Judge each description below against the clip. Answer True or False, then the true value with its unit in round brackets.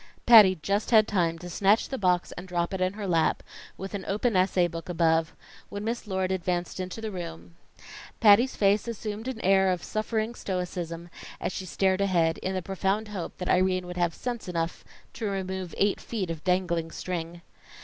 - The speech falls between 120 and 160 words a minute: False (190 wpm)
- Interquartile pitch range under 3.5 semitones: True (2.7 semitones)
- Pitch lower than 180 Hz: False (185 Hz)